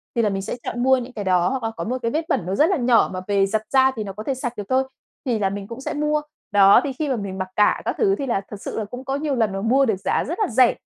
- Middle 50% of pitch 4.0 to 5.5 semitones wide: Yes, average, 4.8 semitones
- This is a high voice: Yes, high, 235 Hz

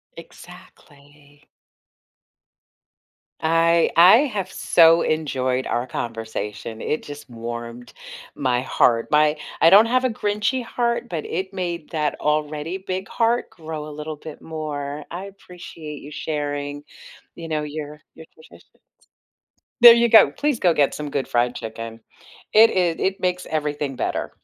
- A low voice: No, medium, 155 Hz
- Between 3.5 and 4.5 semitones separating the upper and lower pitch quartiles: Yes, average, 4.2 semitones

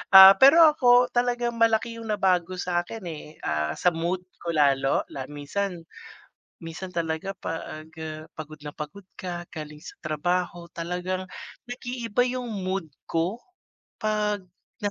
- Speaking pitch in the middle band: Yes, medium, 180 Hz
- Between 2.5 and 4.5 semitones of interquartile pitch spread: No, average, 5.2 semitones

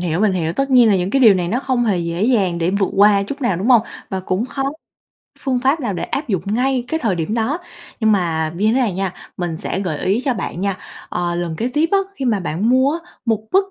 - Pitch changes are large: Yes, wide, 5.9 semitones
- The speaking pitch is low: No, high, 210 Hz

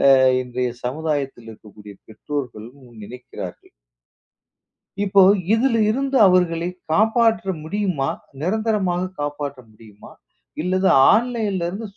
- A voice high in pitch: No, medium, 170 Hz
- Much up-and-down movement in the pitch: Yes, wide, 8.5 semitones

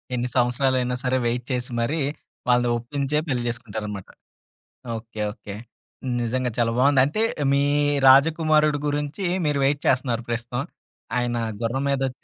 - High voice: No, low, 125 Hz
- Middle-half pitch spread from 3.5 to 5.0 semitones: No, average, 2.8 semitones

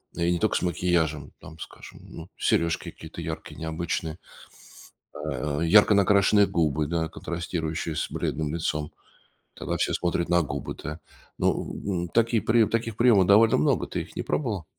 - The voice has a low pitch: Yes, very low, 85 Hz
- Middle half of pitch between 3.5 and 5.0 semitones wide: Yes, average, 4.1 semitones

